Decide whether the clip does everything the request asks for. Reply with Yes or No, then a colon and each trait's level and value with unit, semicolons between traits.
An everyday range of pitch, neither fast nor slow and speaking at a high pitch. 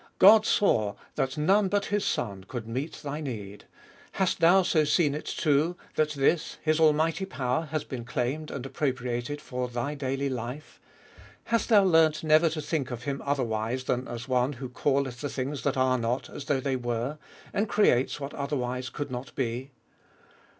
No: average, 3.7 semitones; average, 180 wpm; medium, 140 Hz